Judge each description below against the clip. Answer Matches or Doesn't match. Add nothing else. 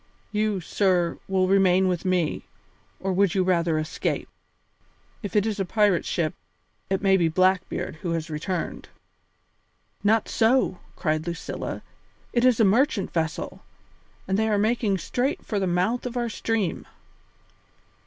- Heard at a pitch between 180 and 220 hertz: Matches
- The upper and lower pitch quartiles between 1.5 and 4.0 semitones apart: Matches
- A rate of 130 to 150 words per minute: Matches